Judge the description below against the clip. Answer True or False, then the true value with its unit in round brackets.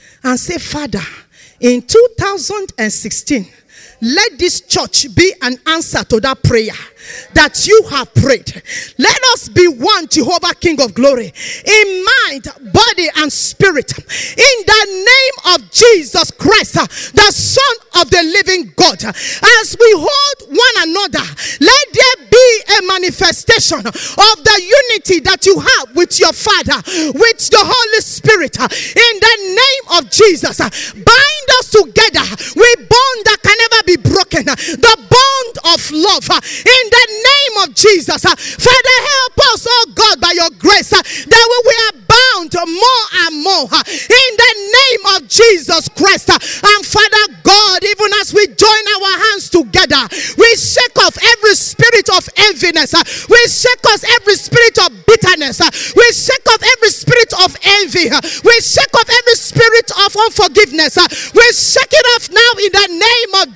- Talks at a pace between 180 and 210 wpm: False (150 wpm)